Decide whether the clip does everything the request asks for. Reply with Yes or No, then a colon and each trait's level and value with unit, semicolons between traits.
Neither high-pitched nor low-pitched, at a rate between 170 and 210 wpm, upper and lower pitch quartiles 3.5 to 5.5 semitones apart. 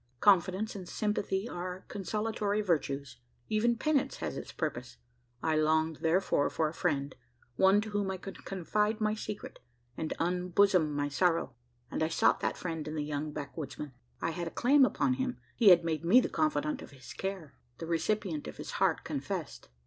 Yes: medium, 180 Hz; average, 180 wpm; average, 5.1 semitones